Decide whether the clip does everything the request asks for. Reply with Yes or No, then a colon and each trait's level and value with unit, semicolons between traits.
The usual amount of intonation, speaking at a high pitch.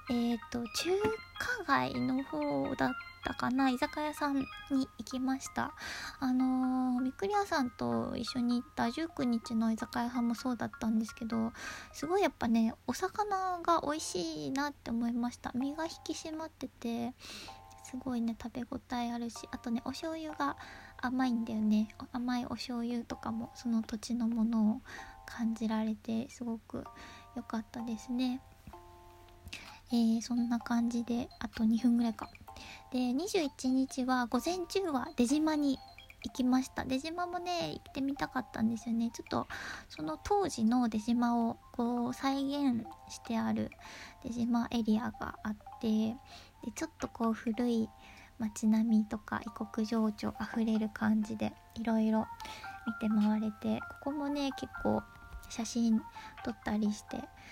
Yes: average, 3.3 semitones; high, 240 Hz